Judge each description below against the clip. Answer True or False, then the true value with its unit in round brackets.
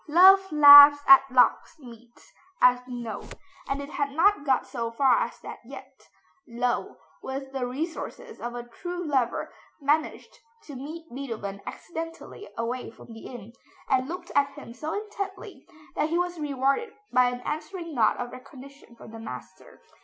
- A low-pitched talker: False (275 Hz)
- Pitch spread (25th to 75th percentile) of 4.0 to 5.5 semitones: True (4.7 semitones)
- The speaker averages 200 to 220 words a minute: False (160 wpm)